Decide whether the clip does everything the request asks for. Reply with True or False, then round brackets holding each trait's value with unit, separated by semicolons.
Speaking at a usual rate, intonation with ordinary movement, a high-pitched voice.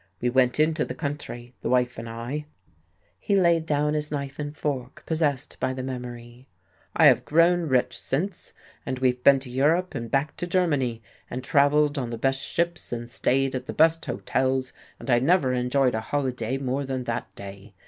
False (190 wpm; 3.3 semitones; 135 Hz)